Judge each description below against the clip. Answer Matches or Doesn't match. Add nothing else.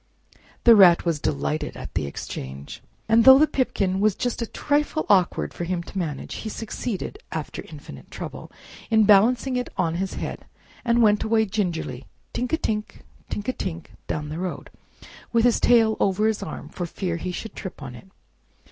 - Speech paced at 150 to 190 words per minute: Matches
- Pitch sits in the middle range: Doesn't match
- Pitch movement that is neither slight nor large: Matches